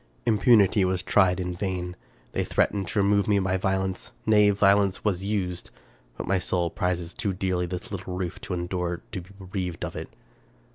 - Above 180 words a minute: Yes, average, 190 wpm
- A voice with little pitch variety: Yes, narrow, 1.9 semitones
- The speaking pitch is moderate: No, very low, 95 Hz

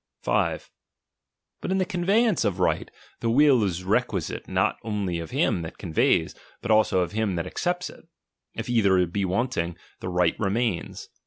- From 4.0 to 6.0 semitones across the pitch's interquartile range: Yes, wide, 5.5 semitones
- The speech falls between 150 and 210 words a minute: Yes, average, 170 wpm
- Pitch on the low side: Yes, low, 100 Hz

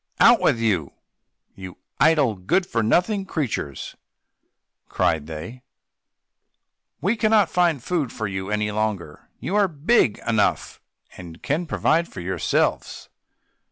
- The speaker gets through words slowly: Yes, slow, 125 wpm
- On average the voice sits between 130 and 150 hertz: No, low, 115 Hz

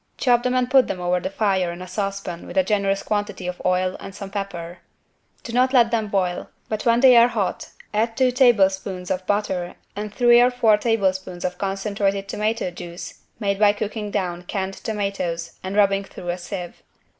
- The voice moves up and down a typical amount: Yes, average, 3.3 semitones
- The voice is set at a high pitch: Yes, high, 200 Hz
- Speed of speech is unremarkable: Yes, average, 190 wpm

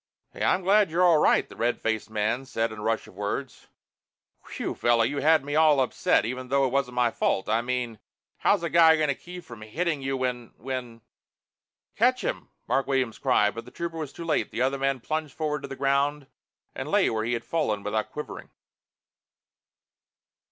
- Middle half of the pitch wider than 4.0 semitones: Yes, average, 4.6 semitones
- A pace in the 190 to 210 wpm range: Yes, fast, 205 wpm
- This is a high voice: No, low, 135 Hz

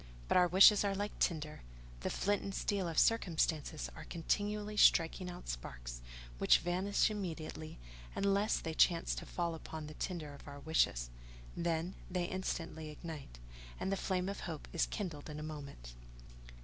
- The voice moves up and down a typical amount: Yes, average, 3.8 semitones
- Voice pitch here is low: No, medium, 170 Hz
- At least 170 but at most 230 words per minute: No, average, 160 wpm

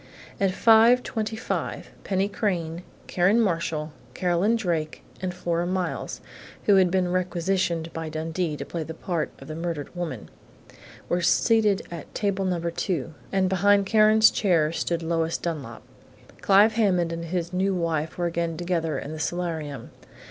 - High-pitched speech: No, medium, 175 Hz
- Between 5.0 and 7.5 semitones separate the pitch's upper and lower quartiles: No, average, 2.9 semitones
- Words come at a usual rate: Yes, average, 150 wpm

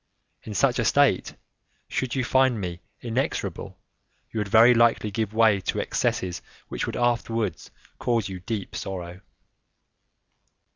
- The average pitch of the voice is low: Yes, low, 110 Hz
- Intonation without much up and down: No, average, 3.5 semitones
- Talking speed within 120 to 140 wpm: Yes, slow, 135 wpm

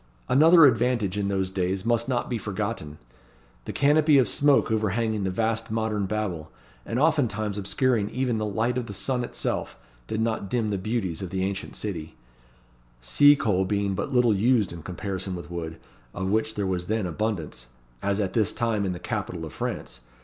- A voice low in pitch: Yes, low, 105 Hz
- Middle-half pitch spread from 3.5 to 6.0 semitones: Yes, average, 3.8 semitones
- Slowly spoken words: No, average, 185 wpm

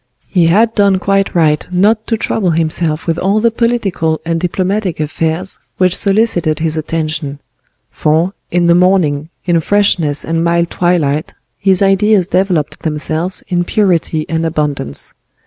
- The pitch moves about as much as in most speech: Yes, average, 3.5 semitones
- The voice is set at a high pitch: No, medium, 175 Hz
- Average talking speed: Yes, average, 145 wpm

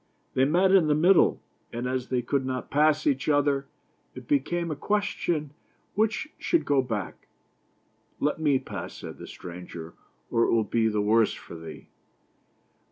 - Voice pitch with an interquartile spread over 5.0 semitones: Yes, wide, 5.4 semitones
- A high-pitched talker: No, medium, 140 Hz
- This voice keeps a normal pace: Yes, average, 170 wpm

